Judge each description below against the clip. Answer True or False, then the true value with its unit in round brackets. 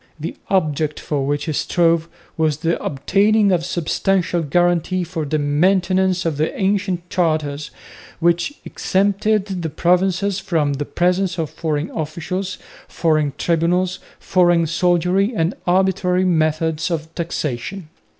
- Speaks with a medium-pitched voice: True (170 Hz)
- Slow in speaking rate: True (125 wpm)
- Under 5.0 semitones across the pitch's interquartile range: True (3.0 semitones)